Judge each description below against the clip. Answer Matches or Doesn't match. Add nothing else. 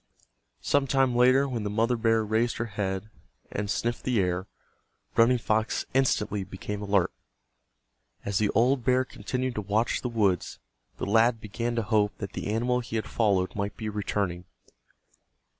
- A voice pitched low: Matches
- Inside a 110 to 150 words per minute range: Doesn't match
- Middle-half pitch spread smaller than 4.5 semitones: Matches